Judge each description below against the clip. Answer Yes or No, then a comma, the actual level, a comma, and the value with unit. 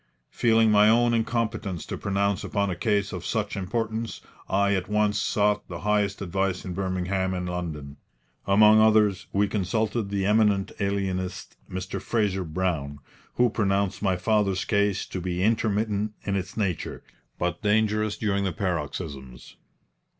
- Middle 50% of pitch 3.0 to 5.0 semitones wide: No, narrow, 2.4 semitones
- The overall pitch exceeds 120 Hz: No, low, 100 Hz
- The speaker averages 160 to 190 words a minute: No, average, 145 wpm